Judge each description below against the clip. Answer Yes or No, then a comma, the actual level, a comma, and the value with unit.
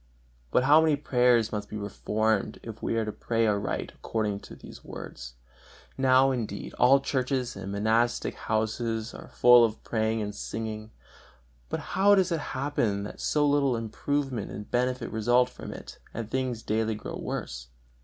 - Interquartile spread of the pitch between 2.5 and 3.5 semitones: Yes, average, 3.2 semitones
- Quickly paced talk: No, average, 165 wpm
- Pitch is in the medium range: No, low, 115 Hz